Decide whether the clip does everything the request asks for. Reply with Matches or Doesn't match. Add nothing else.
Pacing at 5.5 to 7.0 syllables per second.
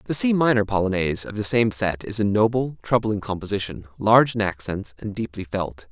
Matches